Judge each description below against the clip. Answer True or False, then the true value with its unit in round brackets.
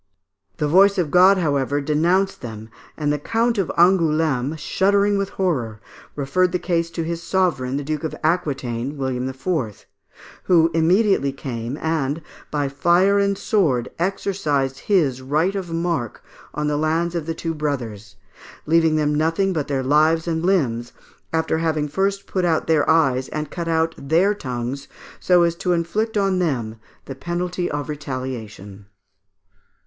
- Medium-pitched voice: True (160 Hz)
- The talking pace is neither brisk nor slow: True (155 wpm)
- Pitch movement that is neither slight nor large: True (4.6 semitones)